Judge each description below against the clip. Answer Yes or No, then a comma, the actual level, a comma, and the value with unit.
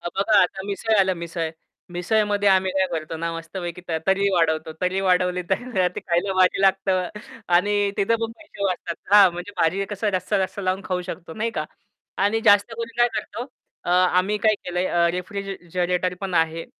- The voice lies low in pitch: No, high, 190 Hz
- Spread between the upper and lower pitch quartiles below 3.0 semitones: Yes, narrow, 2.4 semitones